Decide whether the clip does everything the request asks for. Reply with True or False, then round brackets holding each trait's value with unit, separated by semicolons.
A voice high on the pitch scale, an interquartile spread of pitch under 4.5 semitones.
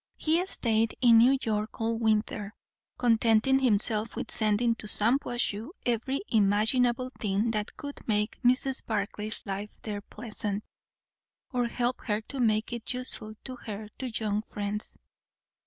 True (225 Hz; 2.6 semitones)